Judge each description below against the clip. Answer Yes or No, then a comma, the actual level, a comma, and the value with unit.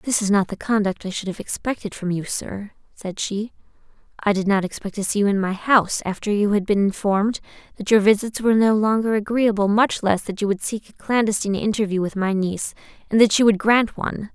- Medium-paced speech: No, fast, 225 wpm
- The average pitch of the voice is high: Yes, high, 205 Hz